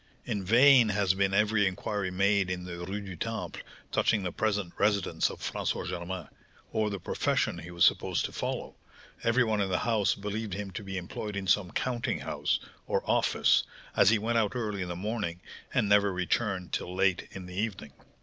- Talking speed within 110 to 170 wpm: No, average, 195 wpm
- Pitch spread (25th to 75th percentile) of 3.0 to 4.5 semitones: No, narrow, 2.6 semitones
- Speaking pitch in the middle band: No, low, 100 Hz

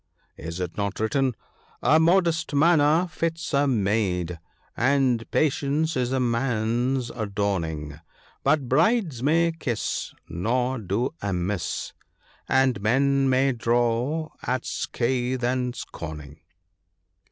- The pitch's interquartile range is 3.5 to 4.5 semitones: No, average, 4.9 semitones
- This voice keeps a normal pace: No, slow, 115 wpm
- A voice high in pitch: No, low, 125 Hz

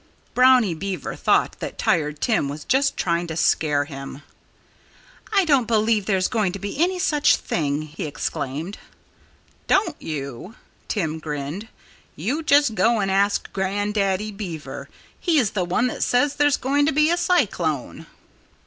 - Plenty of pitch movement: Yes, wide, 8.4 semitones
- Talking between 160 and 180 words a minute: No, average, 150 wpm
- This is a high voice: Yes, high, 200 Hz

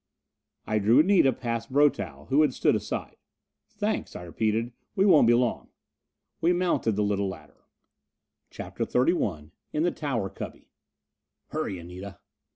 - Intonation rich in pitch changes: Yes, wide, 6.7 semitones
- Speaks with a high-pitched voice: No, low, 115 Hz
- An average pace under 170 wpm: Yes, average, 140 wpm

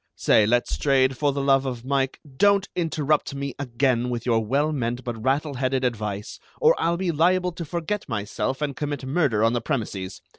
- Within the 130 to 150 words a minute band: No, average, 185 wpm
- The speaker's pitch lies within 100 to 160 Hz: Yes, low, 135 Hz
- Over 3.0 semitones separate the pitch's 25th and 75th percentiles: Yes, average, 4.1 semitones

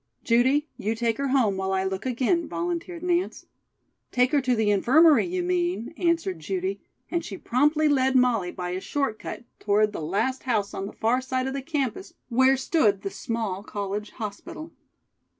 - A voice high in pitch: Yes, very high, 250 Hz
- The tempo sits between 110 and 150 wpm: No, average, 180 wpm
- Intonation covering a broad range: Yes, wide, 6.5 semitones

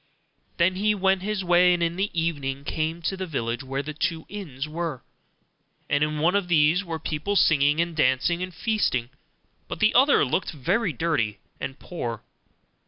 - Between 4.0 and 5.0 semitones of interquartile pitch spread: Yes, average, 4.4 semitones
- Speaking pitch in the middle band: Yes, medium, 165 Hz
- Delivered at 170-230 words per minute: Yes, average, 175 wpm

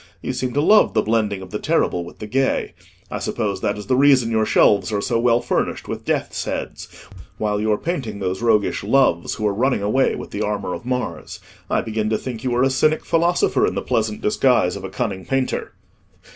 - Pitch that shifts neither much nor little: Yes, average, 3.9 semitones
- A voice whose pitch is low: Yes, low, 110 Hz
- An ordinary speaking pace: No, fast, 220 wpm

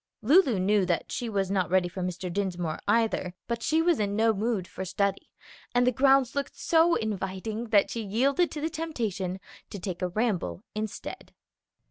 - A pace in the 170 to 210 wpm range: Yes, average, 180 wpm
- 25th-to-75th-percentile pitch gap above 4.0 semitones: Yes, average, 4.6 semitones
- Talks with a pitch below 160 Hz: No, high, 210 Hz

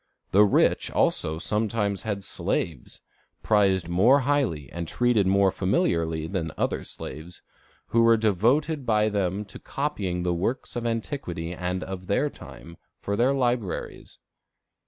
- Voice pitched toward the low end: Yes, low, 100 Hz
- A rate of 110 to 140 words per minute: Yes, slow, 135 wpm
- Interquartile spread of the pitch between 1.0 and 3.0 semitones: No, average, 4.8 semitones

